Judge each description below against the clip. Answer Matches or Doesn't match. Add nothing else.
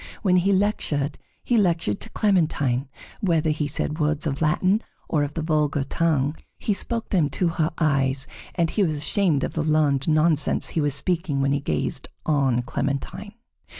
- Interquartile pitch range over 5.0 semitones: Doesn't match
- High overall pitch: Doesn't match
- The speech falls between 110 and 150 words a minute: Doesn't match